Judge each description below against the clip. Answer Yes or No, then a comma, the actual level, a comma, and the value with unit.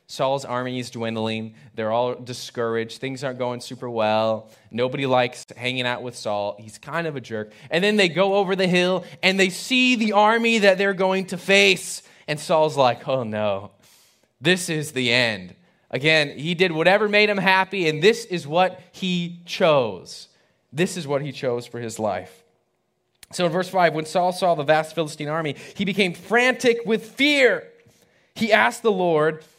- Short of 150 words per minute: No, average, 185 wpm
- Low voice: No, medium, 160 Hz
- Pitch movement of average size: No, wide, 7.4 semitones